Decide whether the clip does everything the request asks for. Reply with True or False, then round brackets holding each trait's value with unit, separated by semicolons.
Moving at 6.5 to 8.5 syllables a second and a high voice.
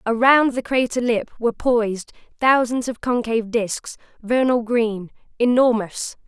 False (4.4 syllables/s; 235 Hz)